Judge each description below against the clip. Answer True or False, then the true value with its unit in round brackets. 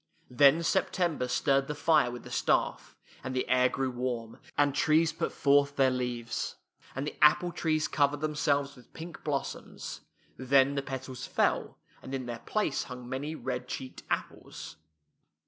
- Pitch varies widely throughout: False (2.8 semitones)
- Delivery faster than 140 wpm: True (165 wpm)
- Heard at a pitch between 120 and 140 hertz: True (135 Hz)